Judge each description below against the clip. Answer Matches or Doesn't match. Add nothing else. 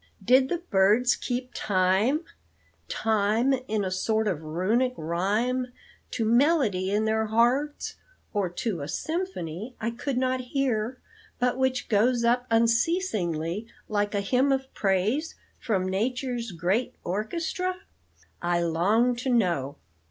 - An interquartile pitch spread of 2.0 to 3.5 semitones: Doesn't match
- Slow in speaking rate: Matches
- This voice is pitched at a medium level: Doesn't match